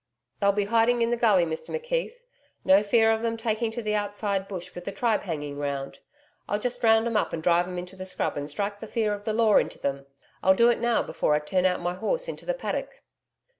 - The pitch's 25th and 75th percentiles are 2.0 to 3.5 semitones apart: No, average, 4.2 semitones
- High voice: Yes, high, 205 Hz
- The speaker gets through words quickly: Yes, fast, 245 wpm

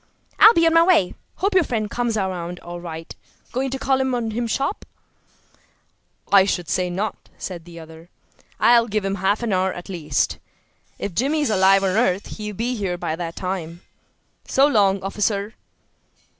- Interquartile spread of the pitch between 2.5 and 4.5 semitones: No, average, 5.2 semitones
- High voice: Yes, high, 200 Hz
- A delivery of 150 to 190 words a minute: Yes, average, 180 wpm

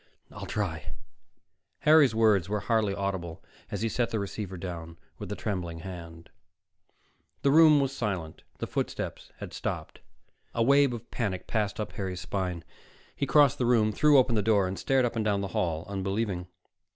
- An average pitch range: Yes, average, 4.4 semitones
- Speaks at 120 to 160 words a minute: No, average, 170 wpm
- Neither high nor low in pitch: No, low, 105 Hz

